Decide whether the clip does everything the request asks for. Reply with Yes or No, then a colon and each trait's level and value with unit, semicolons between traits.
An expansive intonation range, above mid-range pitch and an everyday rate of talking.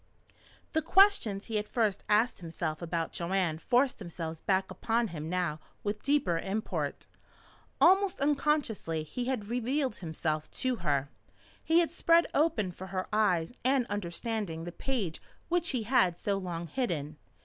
Yes: wide, 7.2 semitones; high, 205 Hz; average, 150 wpm